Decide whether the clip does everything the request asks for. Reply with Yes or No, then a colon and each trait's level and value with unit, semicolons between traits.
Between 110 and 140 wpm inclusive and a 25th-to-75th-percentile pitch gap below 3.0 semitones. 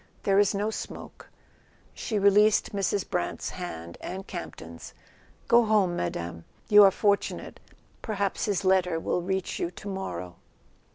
Yes: slow, 135 wpm; narrow, 2.6 semitones